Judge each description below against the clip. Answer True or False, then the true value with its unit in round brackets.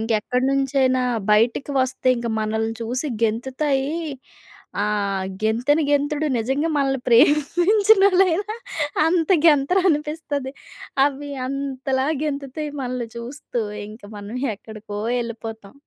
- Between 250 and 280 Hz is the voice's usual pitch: True (270 Hz)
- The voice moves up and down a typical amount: True (4.4 semitones)